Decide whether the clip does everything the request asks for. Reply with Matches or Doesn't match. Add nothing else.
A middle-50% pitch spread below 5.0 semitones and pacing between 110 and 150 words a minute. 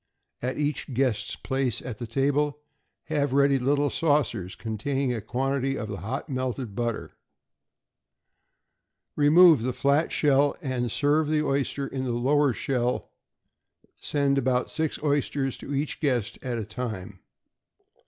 Matches